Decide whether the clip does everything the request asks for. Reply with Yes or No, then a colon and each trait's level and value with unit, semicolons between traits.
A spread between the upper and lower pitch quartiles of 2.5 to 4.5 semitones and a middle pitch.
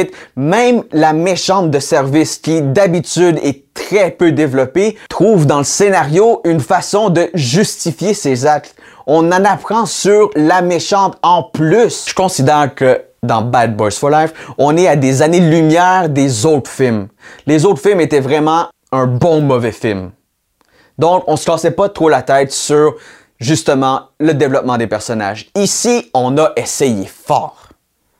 No: average, 4.9 semitones; medium, 155 Hz